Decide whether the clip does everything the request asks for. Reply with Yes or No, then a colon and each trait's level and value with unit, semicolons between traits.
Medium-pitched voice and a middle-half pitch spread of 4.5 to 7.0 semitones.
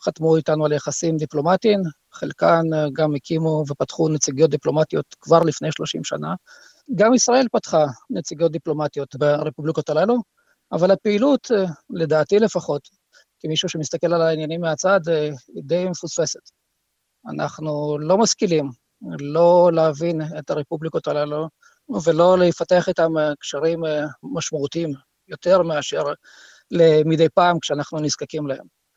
No: medium, 160 Hz; average, 3.0 semitones